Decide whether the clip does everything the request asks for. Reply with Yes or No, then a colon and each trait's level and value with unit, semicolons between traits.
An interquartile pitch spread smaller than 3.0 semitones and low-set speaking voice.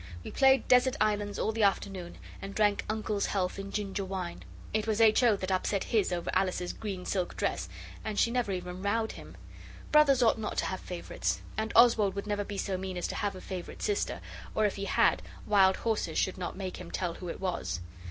No: narrow, 2.6 semitones; high, 200 Hz